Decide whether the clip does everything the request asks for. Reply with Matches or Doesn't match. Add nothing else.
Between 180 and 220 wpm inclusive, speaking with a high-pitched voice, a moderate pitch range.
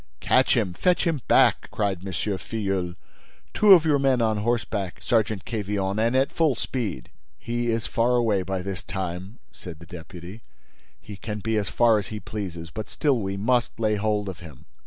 Doesn't match